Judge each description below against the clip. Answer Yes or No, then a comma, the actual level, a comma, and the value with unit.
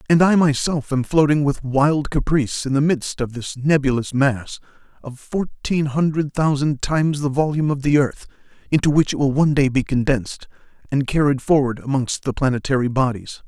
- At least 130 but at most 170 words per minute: No, average, 180 wpm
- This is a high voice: No, medium, 140 Hz